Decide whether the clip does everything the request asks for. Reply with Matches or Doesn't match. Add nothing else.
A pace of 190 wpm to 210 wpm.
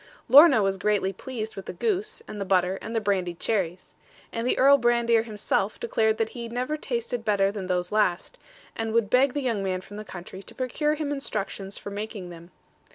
Matches